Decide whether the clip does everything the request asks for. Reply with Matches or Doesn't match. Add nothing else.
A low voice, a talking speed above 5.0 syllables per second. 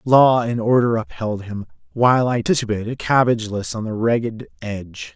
Matches